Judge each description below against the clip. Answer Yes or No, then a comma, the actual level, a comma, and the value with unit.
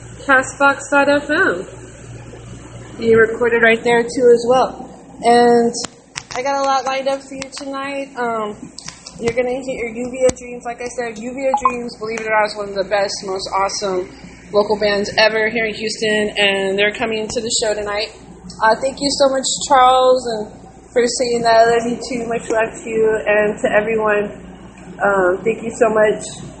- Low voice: No, high, 230 Hz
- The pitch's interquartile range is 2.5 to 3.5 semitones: Yes, average, 3.1 semitones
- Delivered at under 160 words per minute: No, average, 180 wpm